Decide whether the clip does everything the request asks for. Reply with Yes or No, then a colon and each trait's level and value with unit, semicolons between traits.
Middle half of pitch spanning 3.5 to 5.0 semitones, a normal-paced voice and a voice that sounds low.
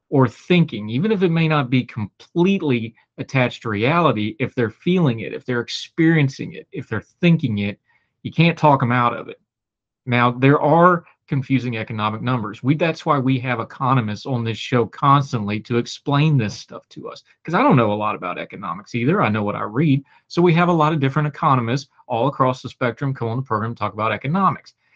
No: average, 4.7 semitones; fast, 210 wpm; low, 130 Hz